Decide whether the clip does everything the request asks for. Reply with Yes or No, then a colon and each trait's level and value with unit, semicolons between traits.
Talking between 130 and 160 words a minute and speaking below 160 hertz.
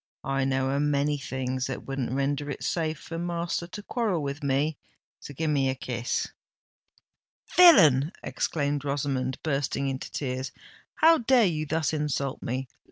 Yes: average, 155 wpm; medium, 140 Hz